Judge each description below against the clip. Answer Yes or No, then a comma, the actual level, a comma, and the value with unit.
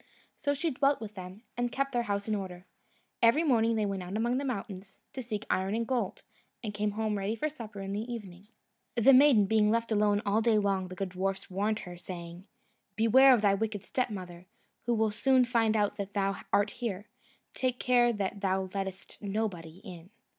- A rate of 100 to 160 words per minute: No, average, 200 wpm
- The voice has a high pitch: Yes, high, 210 Hz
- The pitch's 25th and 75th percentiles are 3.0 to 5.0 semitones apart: Yes, average, 3.3 semitones